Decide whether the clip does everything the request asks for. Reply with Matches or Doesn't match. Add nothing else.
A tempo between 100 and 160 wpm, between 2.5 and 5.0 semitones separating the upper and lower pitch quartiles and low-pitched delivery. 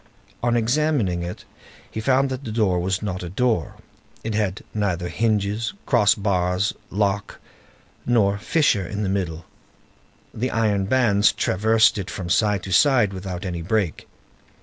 Matches